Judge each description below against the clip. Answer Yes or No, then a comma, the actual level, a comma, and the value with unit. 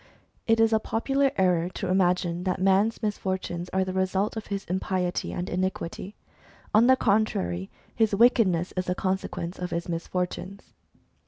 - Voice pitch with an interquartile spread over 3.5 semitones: No, average, 2.9 semitones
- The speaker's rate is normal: Yes, average, 160 wpm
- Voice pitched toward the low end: No, high, 190 Hz